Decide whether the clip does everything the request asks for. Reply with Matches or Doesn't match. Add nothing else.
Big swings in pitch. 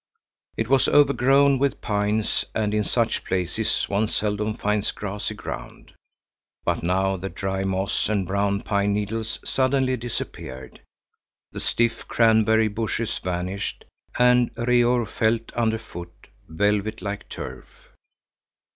Doesn't match